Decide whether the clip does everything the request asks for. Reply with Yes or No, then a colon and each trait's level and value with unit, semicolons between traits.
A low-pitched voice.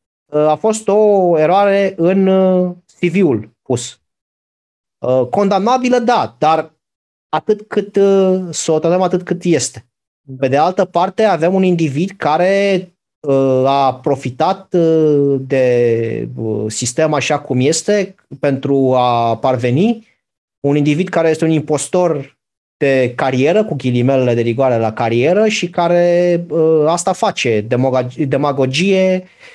No: medium, 155 Hz